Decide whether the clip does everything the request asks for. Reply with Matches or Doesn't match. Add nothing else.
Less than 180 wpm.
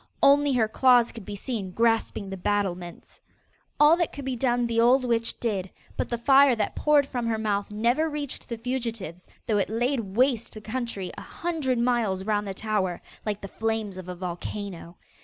Doesn't match